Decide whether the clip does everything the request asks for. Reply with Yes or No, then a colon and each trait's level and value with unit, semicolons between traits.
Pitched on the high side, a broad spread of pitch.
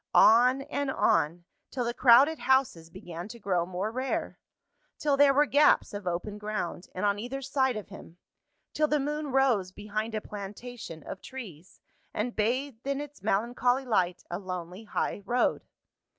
Yes: high, 225 Hz; wide, 5.9 semitones